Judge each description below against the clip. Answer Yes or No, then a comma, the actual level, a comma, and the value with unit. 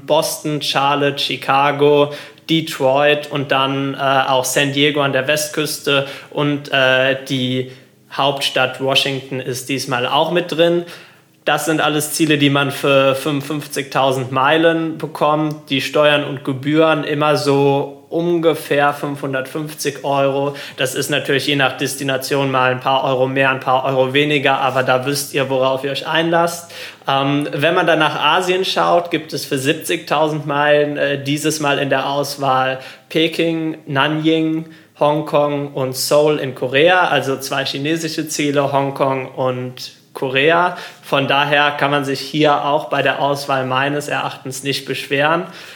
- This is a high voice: No, medium, 140 Hz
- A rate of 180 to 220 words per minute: No, average, 145 wpm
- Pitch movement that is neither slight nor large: No, narrow, 1.9 semitones